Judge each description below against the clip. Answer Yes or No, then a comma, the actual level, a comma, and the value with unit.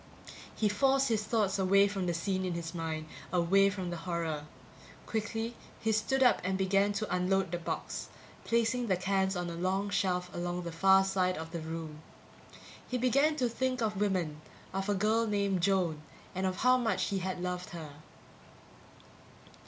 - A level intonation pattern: No, average, 3.4 semitones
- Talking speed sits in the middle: Yes, average, 175 wpm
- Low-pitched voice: No, high, 190 Hz